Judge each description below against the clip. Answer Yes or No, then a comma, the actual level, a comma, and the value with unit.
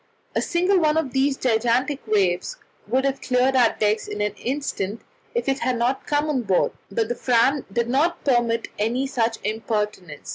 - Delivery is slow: No, average, 175 wpm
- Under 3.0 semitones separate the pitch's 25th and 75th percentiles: No, average, 3.8 semitones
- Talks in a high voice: Yes, high, 245 Hz